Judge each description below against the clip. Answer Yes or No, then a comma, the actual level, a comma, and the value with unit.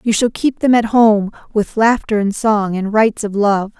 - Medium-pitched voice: No, high, 215 Hz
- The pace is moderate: No, fast, 220 wpm